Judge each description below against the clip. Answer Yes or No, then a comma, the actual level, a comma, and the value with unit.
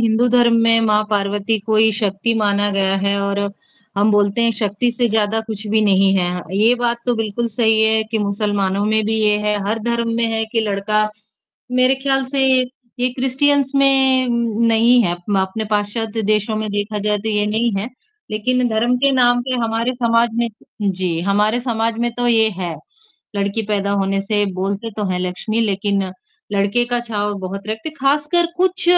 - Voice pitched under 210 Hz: No, high, 220 Hz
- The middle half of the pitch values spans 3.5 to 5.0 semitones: No, average, 2.7 semitones